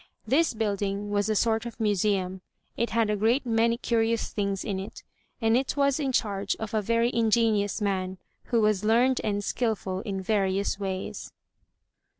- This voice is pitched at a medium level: No, high, 215 Hz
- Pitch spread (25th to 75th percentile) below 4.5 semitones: Yes, narrow, 2.6 semitones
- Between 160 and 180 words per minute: Yes, average, 165 wpm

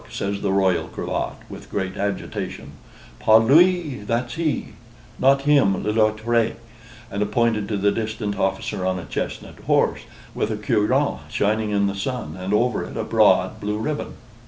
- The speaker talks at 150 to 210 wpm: Yes, average, 160 wpm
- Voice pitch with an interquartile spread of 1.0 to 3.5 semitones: Yes, average, 2.8 semitones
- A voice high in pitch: No, low, 105 Hz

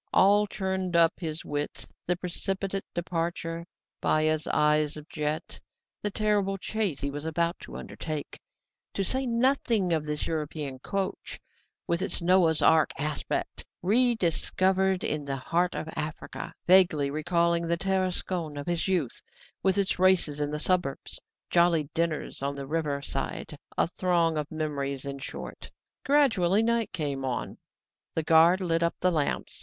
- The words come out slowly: No, average, 150 wpm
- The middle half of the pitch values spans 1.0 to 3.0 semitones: No, average, 3.8 semitones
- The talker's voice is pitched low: No, medium, 170 Hz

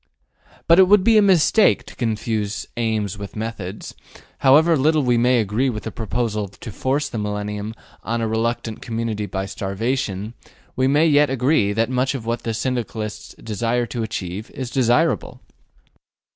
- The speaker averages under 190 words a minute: Yes, average, 160 wpm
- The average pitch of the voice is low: Yes, low, 115 Hz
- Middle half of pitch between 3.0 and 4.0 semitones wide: Yes, average, 3.7 semitones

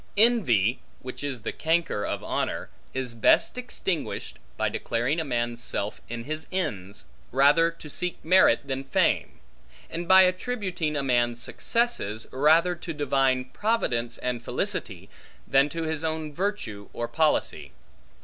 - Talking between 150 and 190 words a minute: No, average, 140 wpm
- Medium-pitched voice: Yes, medium, 145 Hz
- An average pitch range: No, wide, 6.1 semitones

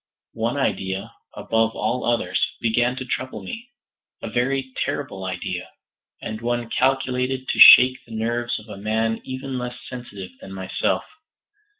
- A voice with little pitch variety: No, average, 3.0 semitones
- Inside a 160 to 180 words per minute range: No, average, 140 wpm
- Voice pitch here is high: No, low, 120 Hz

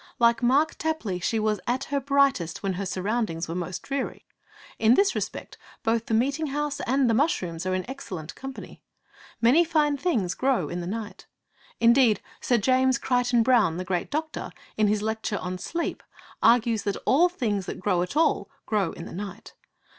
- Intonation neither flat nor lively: No, wide, 6.1 semitones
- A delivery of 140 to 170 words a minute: No, average, 180 wpm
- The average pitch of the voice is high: Yes, high, 230 Hz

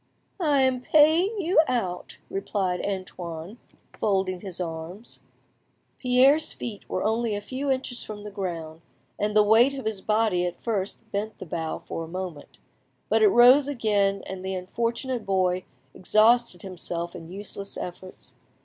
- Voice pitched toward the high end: Yes, high, 205 Hz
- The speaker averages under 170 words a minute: Yes, average, 150 wpm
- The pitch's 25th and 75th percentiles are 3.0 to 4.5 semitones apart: No, average, 4.9 semitones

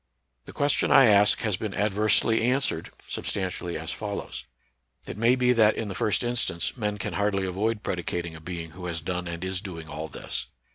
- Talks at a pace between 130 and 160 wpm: No, average, 200 wpm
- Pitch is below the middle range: Yes, low, 100 Hz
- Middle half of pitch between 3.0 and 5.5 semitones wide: Yes, average, 3.9 semitones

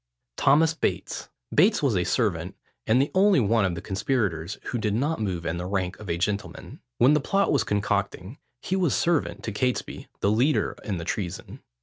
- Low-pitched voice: Yes, low, 110 Hz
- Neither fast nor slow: Yes, average, 195 wpm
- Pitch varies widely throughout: Yes, wide, 6.6 semitones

